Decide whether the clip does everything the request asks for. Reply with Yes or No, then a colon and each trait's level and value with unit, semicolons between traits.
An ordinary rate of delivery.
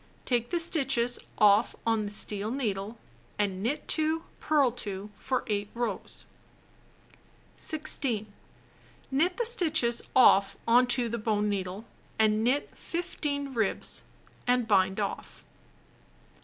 No: slow, 120 wpm